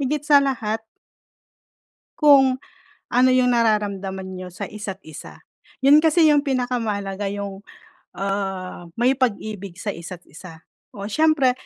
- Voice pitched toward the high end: Yes, high, 215 Hz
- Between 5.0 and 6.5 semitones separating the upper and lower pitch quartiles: Yes, average, 5.3 semitones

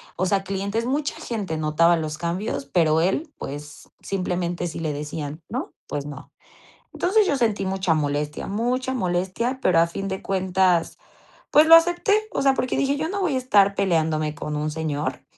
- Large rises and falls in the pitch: Yes, wide, 7.6 semitones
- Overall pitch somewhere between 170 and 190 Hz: Yes, medium, 185 Hz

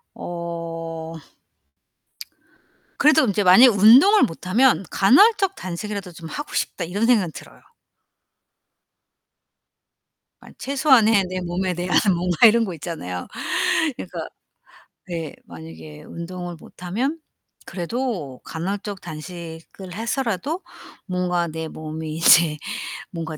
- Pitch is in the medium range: Yes, medium, 180 Hz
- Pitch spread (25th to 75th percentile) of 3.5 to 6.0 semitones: Yes, wide, 5.4 semitones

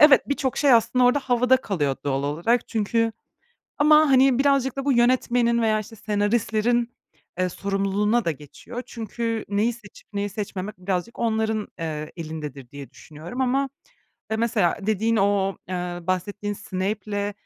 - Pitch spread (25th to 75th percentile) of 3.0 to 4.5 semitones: Yes, average, 4.2 semitones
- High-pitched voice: Yes, high, 215 Hz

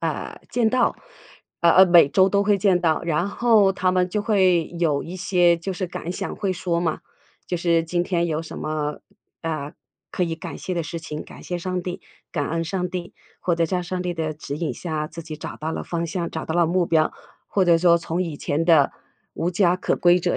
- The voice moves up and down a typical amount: No, narrow, 2.0 semitones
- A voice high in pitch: No, medium, 175 Hz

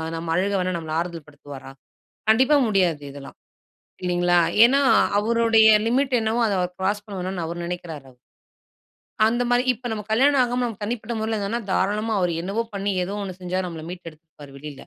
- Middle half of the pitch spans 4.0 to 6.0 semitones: Yes, average, 4.6 semitones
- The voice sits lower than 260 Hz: Yes, high, 190 Hz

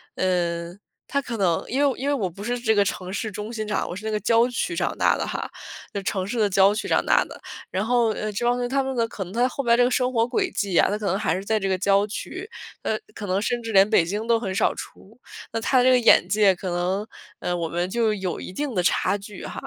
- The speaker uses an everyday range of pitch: Yes, average, 3.9 semitones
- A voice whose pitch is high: Yes, high, 210 Hz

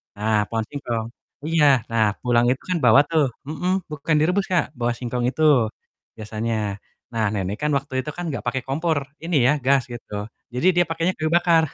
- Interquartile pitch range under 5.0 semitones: No, wide, 5.6 semitones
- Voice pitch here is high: No, low, 135 Hz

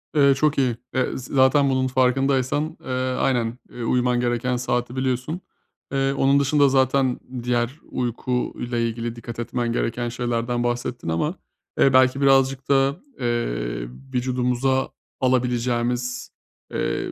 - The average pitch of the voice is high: No, low, 125 Hz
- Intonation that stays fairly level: Yes, narrow, 1.8 semitones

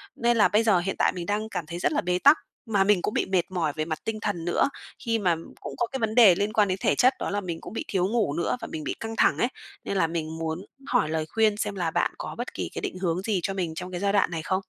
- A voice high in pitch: Yes, high, 195 Hz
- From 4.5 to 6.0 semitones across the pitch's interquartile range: No, average, 4.0 semitones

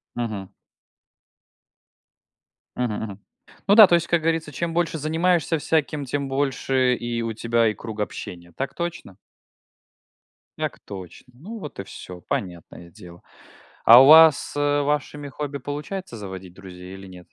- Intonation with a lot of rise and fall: Yes, wide, 7.5 semitones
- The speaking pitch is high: No, low, 130 Hz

